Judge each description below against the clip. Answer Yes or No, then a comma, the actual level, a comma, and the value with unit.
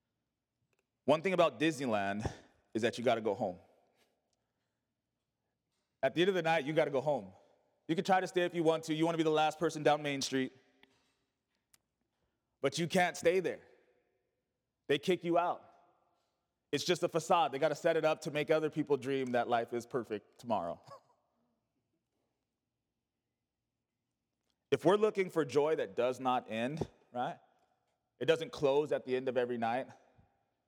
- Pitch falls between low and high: Yes, medium, 155 Hz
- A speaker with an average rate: Yes, average, 165 wpm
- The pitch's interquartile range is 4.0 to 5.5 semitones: Yes, average, 4.6 semitones